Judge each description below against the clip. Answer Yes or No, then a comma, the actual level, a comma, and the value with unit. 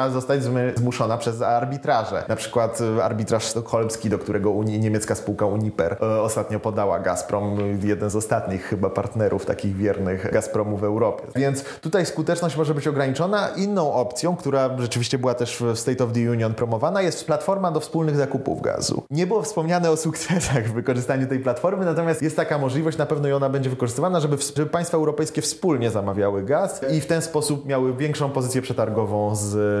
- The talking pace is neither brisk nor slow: No, fast, 175 wpm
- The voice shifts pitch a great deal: Yes, wide, 5.9 semitones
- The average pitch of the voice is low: Yes, low, 130 Hz